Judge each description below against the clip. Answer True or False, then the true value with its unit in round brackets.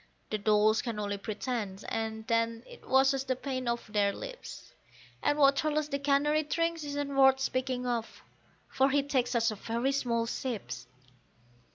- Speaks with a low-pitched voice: False (255 Hz)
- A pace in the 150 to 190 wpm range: True (160 wpm)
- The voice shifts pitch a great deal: False (3.9 semitones)